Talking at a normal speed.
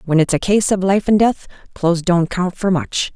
No: fast, 245 wpm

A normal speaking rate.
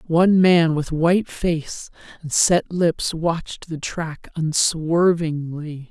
No: slow, 120 wpm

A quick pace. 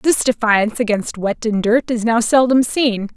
No: average, 190 wpm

